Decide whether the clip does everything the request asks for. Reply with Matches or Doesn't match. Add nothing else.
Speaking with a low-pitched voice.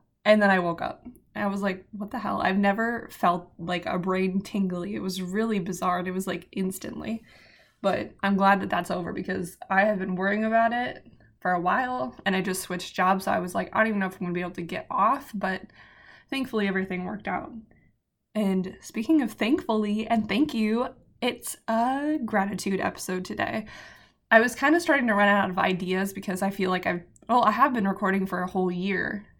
Doesn't match